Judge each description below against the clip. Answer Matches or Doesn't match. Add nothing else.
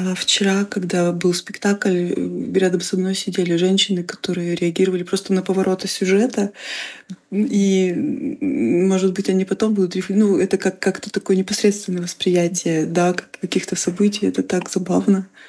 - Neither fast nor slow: Matches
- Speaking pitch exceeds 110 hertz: Matches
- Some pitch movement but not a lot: Doesn't match